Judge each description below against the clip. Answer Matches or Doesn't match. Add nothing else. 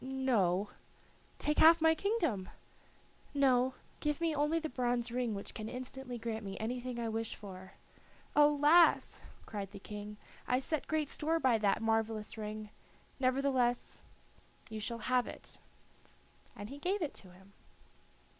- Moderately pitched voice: Doesn't match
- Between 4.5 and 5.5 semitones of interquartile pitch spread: Matches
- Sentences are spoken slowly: Doesn't match